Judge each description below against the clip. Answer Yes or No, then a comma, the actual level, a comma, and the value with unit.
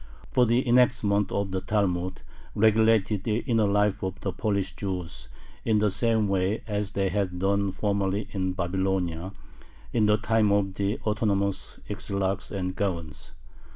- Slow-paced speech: No, average, 150 wpm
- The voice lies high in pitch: No, low, 100 Hz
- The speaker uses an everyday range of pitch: No, narrow, 2.1 semitones